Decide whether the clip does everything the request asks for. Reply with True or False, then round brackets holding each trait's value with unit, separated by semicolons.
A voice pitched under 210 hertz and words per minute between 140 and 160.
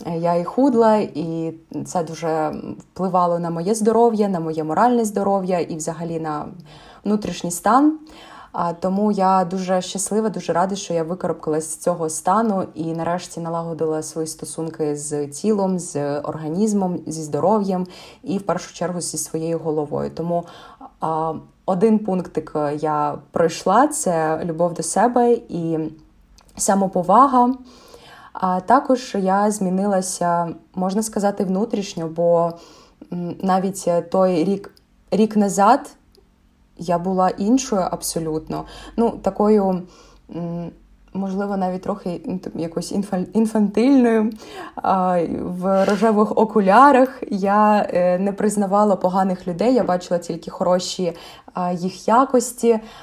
False (185 Hz; 110 wpm)